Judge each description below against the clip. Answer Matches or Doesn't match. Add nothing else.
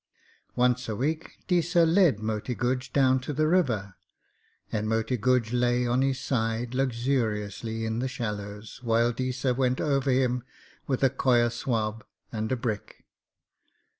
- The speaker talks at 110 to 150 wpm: Matches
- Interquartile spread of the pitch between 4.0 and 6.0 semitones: Doesn't match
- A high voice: Doesn't match